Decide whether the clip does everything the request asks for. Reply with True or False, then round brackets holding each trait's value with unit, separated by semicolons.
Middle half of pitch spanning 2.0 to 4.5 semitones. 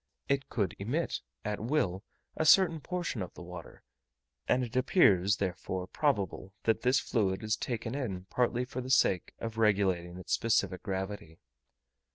False (5.3 semitones)